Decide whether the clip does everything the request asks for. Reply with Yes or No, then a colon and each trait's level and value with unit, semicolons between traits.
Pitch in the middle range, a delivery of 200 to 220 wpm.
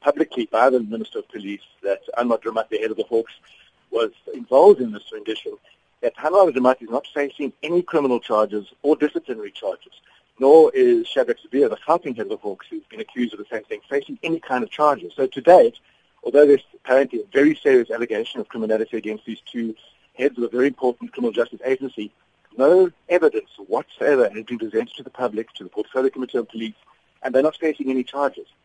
Yes: medium, 145 Hz; fast, 205 wpm